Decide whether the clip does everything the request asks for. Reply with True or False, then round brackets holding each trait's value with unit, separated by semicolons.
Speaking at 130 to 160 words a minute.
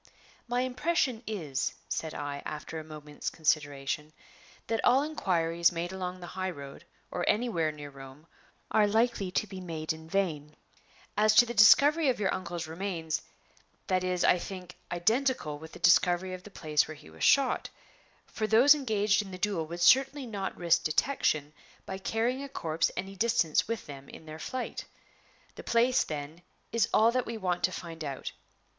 False (175 wpm)